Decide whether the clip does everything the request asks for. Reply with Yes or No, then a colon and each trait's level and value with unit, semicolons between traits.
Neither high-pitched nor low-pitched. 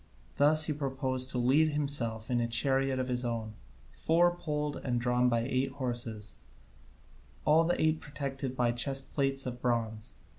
No: low, 130 Hz